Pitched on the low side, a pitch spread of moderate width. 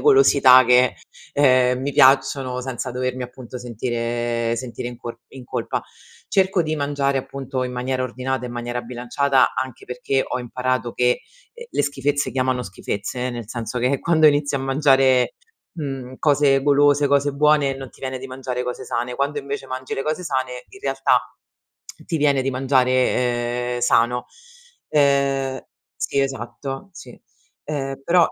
No: low, 130 Hz; narrow, 2.1 semitones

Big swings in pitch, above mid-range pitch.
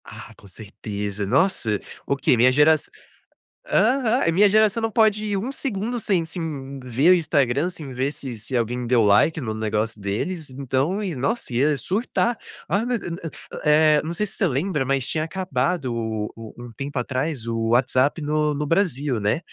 No: wide, 7.0 semitones; medium, 145 Hz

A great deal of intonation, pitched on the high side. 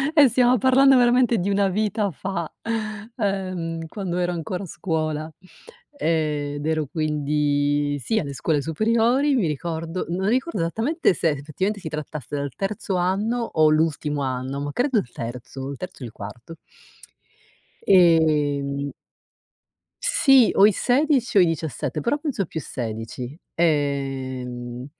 No: wide, 6.2 semitones; medium, 165 Hz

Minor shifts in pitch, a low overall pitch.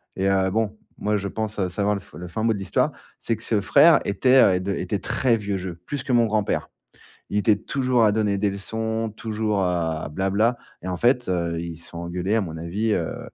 No: average, 3.3 semitones; low, 100 Hz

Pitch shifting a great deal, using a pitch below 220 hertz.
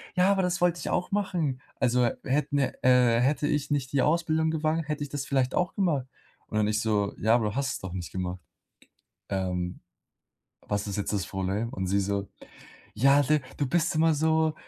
Yes: wide, 7.1 semitones; low, 135 Hz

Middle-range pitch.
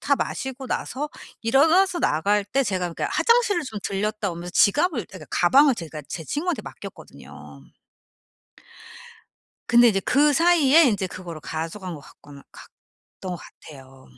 No: high, 205 Hz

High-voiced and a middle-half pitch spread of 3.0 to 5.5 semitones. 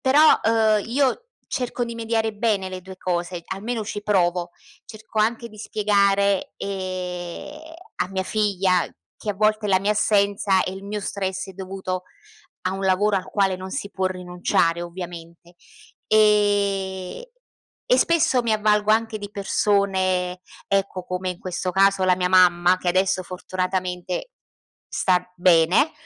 No: high, 195 Hz; narrow, 2.5 semitones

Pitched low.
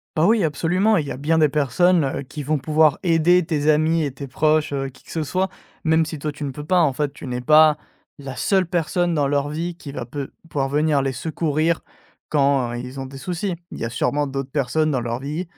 No: medium, 150 Hz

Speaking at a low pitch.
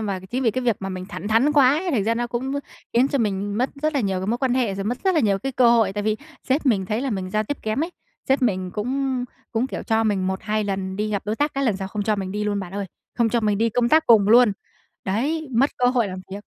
No: high, 225 Hz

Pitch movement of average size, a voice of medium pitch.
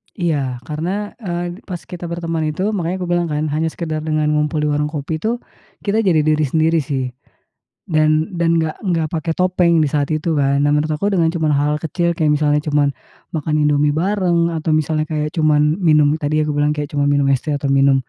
No: narrow, 2.2 semitones; medium, 155 Hz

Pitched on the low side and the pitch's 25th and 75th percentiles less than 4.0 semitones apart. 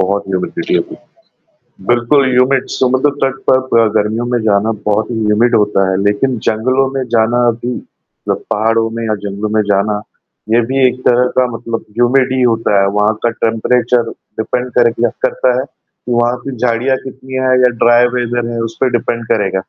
Yes: low, 120 Hz; narrow, 2.4 semitones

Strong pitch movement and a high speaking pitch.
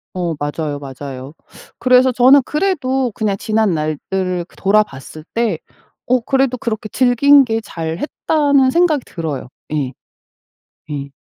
Yes: wide, 8.7 semitones; high, 215 Hz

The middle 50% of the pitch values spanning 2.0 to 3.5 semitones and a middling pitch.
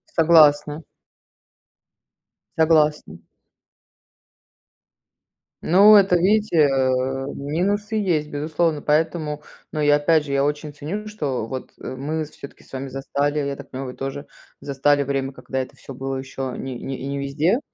Yes: average, 2.9 semitones; medium, 145 Hz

